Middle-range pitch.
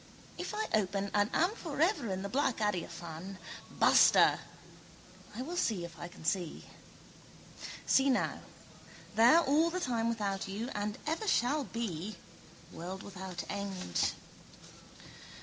No: high, 210 Hz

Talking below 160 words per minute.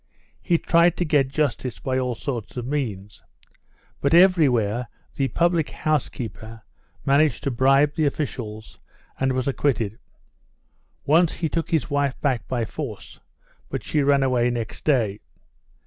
Yes: average, 145 wpm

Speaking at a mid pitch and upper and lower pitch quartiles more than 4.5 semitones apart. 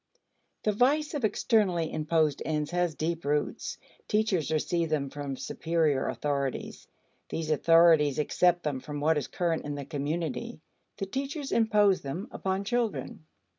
Yes: medium, 165 Hz; average, 4.9 semitones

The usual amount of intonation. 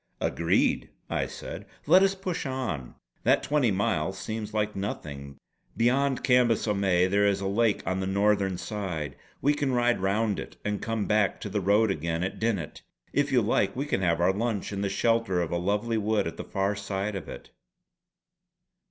Yes: average, 3.2 semitones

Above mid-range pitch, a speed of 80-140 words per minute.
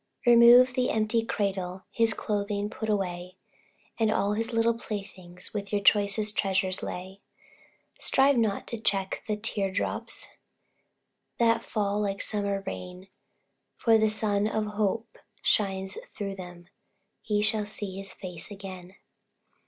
Yes: high, 205 Hz; slow, 135 wpm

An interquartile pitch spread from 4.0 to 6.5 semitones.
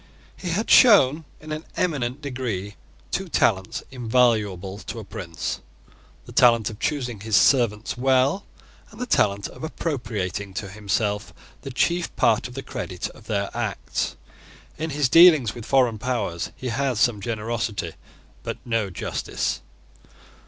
Yes: average, 5.0 semitones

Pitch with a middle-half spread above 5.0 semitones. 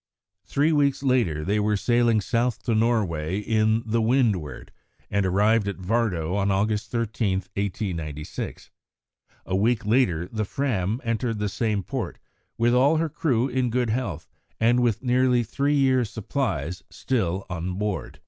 No: average, 4.1 semitones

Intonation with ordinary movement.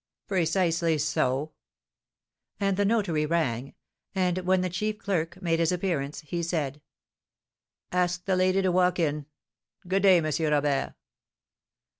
Yes: average, 3.4 semitones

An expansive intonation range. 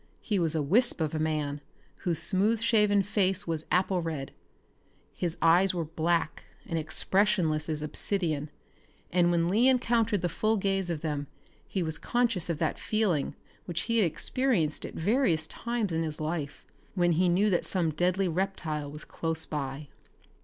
No: average, 4.3 semitones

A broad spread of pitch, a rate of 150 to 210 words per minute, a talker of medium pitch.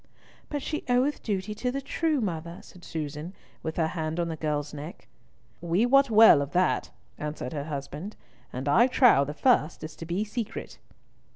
Yes: wide, 7.2 semitones; average, 180 wpm; medium, 170 Hz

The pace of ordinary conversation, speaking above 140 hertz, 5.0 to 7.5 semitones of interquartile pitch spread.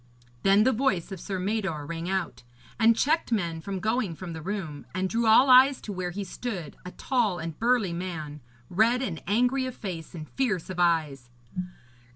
Yes: average, 190 wpm; high, 190 Hz; average, 5.3 semitones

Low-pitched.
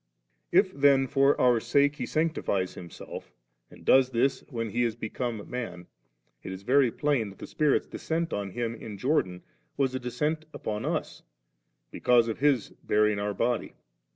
Yes: low, 120 Hz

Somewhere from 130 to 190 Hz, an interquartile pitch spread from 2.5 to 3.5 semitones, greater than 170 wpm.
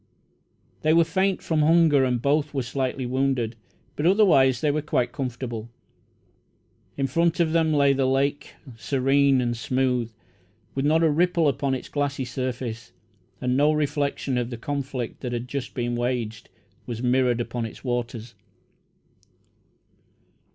No: low, 135 Hz; average, 3.1 semitones; average, 145 wpm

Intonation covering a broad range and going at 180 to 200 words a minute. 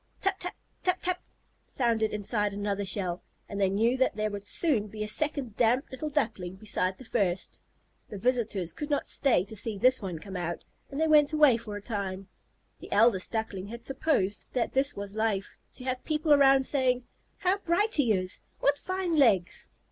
Yes: wide, 5.7 semitones; average, 190 wpm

